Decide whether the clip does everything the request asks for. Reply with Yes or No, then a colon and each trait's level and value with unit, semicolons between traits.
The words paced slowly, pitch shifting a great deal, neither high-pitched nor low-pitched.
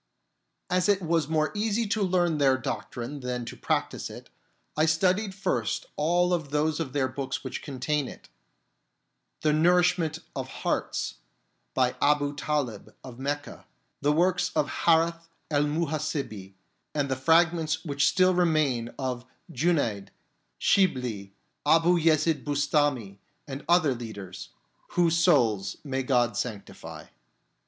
No: slow, 130 wpm; average, 4.3 semitones; medium, 150 Hz